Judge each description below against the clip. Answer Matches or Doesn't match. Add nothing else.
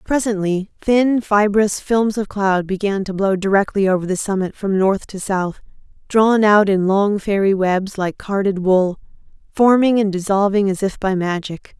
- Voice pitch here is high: Matches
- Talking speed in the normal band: Matches